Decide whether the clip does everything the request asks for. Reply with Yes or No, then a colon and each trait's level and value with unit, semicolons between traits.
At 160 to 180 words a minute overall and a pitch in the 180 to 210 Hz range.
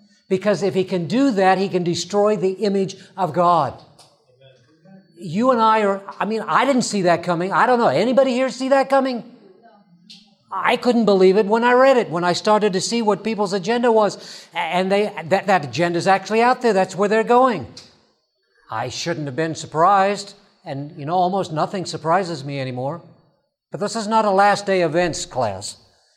No: average, 195 wpm; high, 190 Hz